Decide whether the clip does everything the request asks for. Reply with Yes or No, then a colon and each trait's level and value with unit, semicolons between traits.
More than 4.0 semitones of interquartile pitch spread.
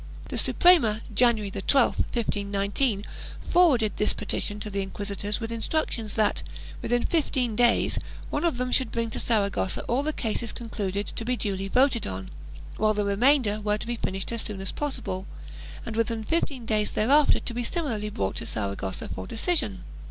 No: average, 3.5 semitones